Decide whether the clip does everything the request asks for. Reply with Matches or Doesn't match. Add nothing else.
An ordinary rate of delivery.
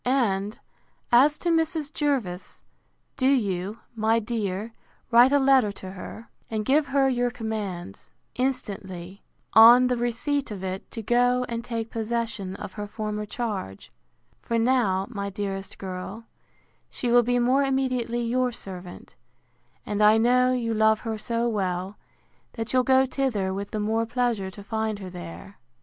Matches